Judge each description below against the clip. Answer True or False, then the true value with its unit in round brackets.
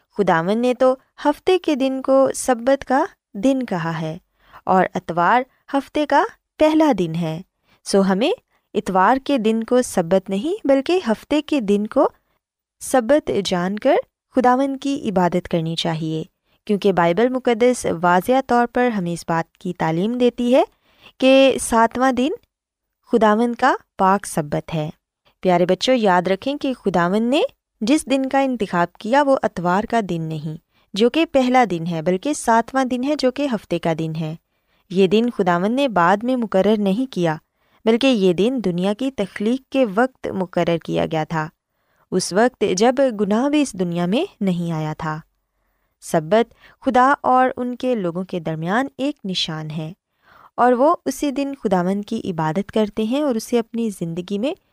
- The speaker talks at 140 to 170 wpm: True (165 wpm)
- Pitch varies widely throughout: True (6.6 semitones)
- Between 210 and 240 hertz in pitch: True (220 Hz)